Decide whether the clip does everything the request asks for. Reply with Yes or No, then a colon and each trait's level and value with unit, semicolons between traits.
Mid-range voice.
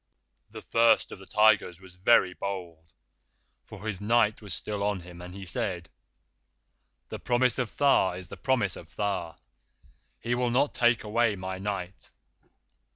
No: low, 100 Hz